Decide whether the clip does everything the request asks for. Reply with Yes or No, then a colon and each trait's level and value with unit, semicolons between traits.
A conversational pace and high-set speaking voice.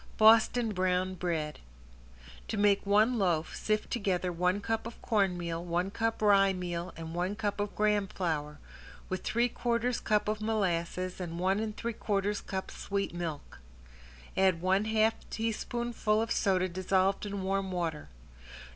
Yes: average, 150 wpm; high, 195 Hz